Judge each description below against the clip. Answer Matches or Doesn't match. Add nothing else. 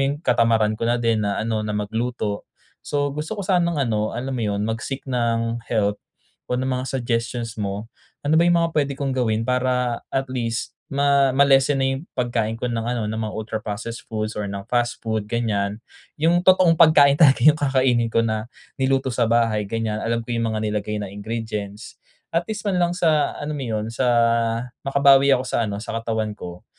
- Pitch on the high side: Doesn't match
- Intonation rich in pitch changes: Doesn't match